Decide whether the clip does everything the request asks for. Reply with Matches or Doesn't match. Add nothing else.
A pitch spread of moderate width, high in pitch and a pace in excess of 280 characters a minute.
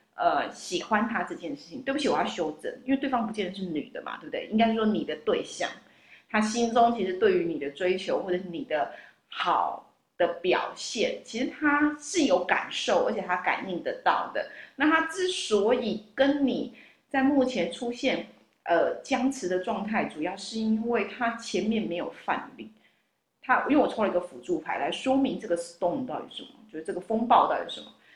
Matches